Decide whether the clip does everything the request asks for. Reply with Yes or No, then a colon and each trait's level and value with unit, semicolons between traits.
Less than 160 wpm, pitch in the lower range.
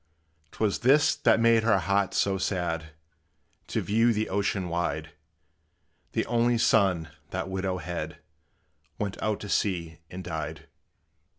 Yes: slow, 135 wpm; very low, 95 Hz